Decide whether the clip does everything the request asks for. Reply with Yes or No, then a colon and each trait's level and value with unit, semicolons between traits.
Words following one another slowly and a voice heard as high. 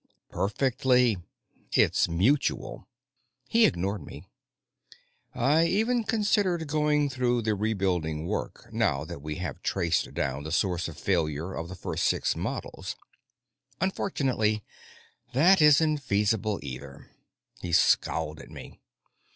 No: slow, 120 wpm; low, 105 Hz